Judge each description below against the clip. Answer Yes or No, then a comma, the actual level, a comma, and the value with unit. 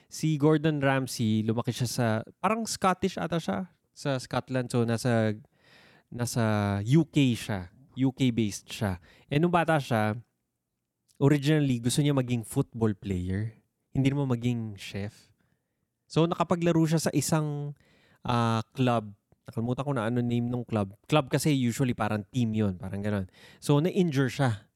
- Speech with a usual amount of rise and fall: Yes, average, 4.9 semitones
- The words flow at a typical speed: Yes, average, 140 wpm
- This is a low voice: Yes, low, 125 Hz